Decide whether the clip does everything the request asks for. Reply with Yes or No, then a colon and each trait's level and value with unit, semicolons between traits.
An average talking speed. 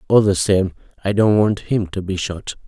No: fast, 225 wpm